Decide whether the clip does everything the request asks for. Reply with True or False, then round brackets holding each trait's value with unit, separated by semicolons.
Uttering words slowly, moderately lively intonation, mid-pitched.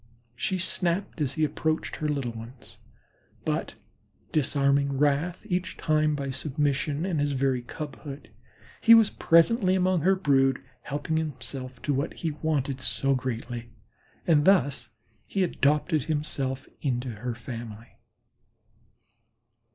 True (130 wpm; 3.3 semitones; 145 Hz)